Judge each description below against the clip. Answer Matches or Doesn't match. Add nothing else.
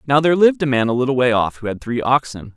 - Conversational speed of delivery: Doesn't match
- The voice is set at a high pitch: Doesn't match